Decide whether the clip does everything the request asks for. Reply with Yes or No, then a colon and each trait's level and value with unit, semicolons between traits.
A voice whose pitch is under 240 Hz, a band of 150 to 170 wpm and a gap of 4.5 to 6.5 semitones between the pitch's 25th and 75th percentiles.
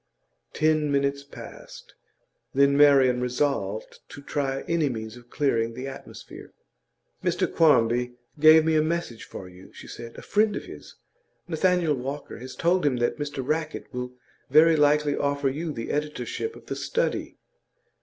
No: medium, 140 Hz; average, 155 wpm; average, 3.8 semitones